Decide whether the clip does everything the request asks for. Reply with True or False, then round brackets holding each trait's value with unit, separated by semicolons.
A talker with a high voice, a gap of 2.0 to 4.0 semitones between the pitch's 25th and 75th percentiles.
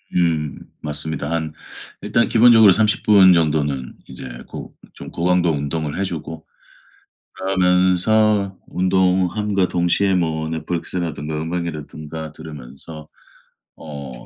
False (85 Hz; 3.4 semitones)